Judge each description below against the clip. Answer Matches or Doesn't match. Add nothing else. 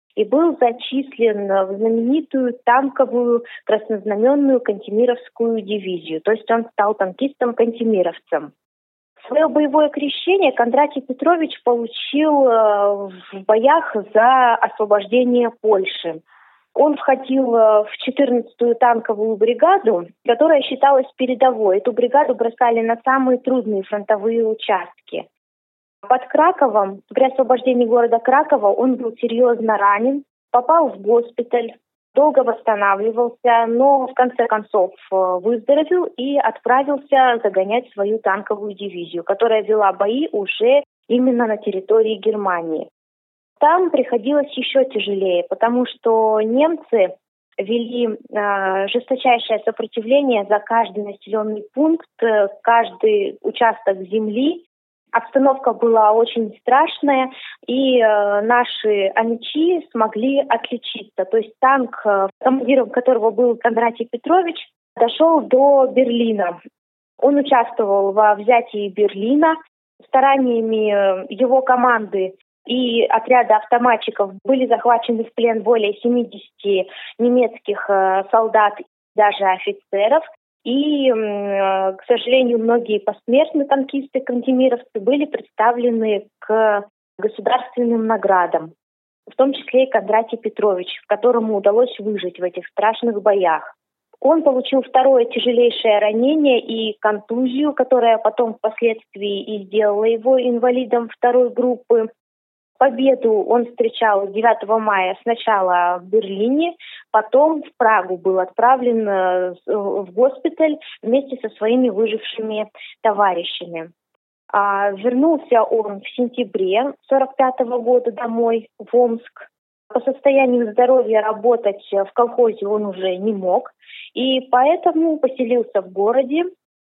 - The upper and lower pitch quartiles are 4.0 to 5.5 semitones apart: Doesn't match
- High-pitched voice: Matches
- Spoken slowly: Matches